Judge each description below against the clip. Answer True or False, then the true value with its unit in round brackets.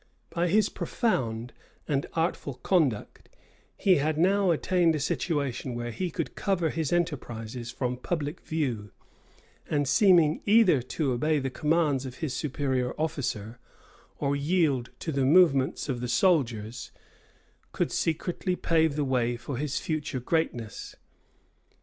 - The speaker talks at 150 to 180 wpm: False (135 wpm)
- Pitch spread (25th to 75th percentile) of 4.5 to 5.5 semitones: True (4.8 semitones)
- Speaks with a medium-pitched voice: True (145 Hz)